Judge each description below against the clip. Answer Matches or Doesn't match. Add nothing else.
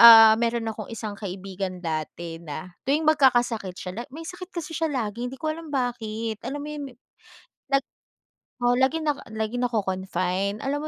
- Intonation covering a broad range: Matches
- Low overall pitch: Doesn't match